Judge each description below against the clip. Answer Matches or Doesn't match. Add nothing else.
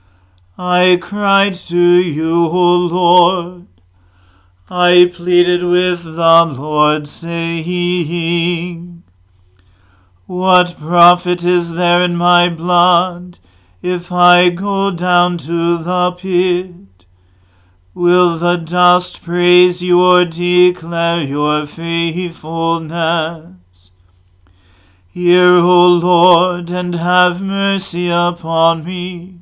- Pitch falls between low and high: Matches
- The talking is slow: Matches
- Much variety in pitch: Doesn't match